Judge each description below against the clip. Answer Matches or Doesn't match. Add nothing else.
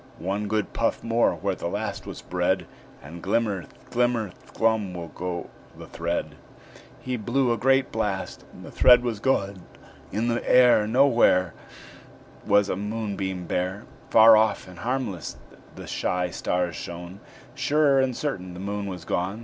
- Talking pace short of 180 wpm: Matches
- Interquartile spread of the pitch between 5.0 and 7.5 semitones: Doesn't match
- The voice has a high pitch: Doesn't match